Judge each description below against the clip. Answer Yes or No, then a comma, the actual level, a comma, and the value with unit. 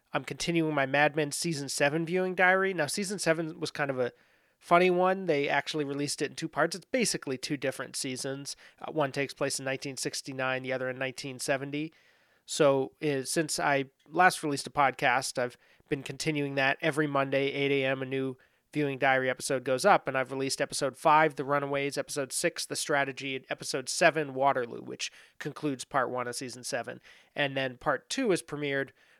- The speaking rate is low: No, average, 185 wpm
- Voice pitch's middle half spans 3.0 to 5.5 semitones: No, narrow, 2.6 semitones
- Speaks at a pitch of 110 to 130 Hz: No, medium, 140 Hz